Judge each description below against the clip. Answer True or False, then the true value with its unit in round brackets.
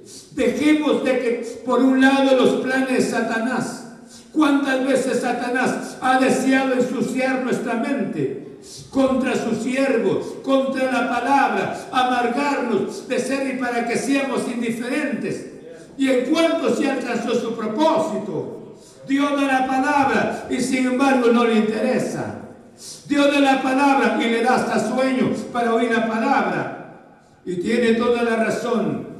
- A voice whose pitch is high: True (250 Hz)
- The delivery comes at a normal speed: True (140 wpm)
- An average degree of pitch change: False (2.2 semitones)